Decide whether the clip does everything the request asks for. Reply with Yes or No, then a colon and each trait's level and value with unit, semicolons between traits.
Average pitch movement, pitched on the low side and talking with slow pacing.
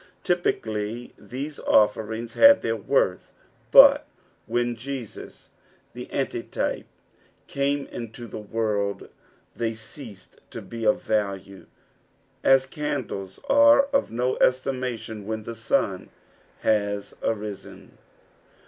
Yes: average, 4.2 semitones; low, 115 Hz; slow, 105 wpm